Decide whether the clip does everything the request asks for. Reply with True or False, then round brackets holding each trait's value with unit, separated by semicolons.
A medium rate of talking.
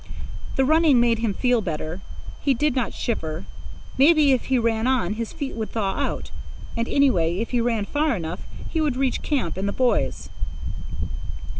True (175 wpm)